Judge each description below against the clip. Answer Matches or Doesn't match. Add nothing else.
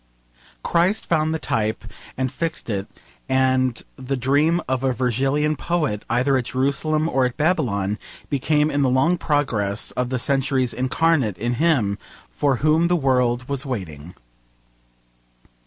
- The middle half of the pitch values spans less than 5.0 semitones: Matches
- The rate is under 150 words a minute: Matches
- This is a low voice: Matches